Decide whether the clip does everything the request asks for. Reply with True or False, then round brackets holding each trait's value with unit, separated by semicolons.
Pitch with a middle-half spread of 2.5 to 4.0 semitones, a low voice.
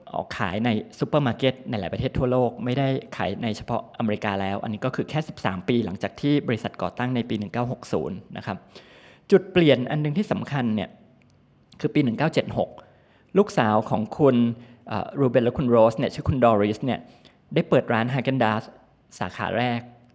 True (3.5 semitones; 120 Hz)